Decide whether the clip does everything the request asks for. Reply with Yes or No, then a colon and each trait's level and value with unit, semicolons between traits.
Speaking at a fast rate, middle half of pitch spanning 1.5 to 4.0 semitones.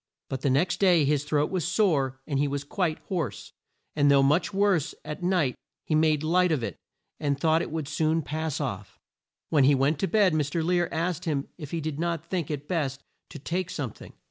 Yes: fast, 215 wpm; average, 3.3 semitones